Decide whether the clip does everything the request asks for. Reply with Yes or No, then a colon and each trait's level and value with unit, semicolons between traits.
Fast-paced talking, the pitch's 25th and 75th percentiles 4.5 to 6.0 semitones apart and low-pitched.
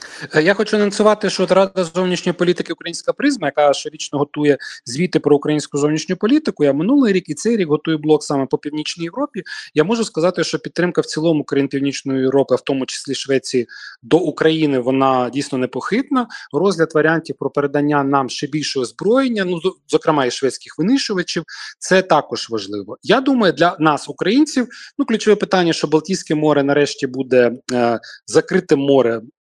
No: fast, 165 wpm; average, 5.0 semitones; medium, 155 Hz